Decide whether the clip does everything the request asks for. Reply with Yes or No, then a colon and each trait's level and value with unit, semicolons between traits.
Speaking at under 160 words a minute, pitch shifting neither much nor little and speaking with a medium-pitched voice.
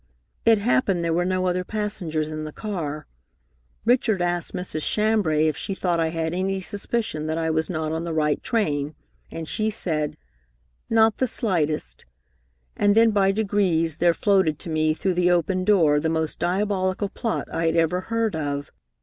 No: average, 175 wpm; average, 4.4 semitones; medium, 175 Hz